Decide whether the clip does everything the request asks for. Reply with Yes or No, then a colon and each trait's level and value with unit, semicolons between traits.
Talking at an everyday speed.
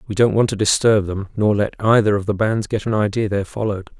No: fast, 270 wpm